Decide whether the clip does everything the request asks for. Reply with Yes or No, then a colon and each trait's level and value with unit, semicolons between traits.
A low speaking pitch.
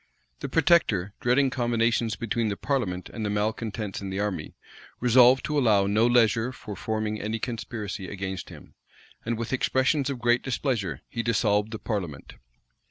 Yes: low, 110 Hz